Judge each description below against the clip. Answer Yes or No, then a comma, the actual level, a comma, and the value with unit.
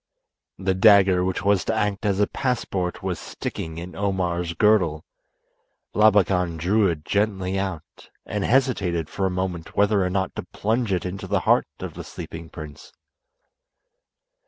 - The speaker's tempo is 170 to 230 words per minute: No, average, 155 wpm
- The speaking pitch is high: No, very low, 95 Hz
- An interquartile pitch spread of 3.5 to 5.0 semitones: No, narrow, 2.6 semitones